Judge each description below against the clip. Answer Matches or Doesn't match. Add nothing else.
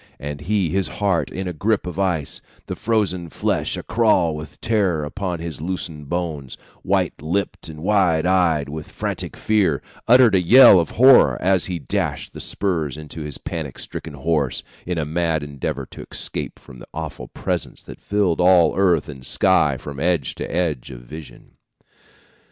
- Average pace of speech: Matches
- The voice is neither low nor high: Doesn't match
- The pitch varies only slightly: Doesn't match